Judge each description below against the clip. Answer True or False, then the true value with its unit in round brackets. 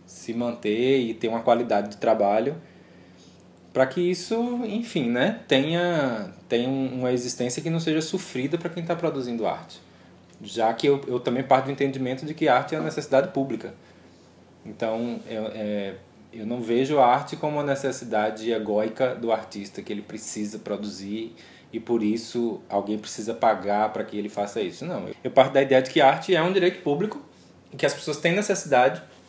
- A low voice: True (120 Hz)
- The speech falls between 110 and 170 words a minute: False (180 wpm)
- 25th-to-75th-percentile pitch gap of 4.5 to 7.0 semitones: True (4.8 semitones)